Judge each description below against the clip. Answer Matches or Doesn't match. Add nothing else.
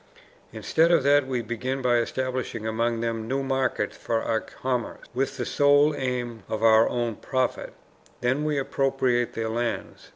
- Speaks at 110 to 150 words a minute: Doesn't match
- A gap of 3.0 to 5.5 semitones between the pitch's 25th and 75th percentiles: Doesn't match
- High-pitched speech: Doesn't match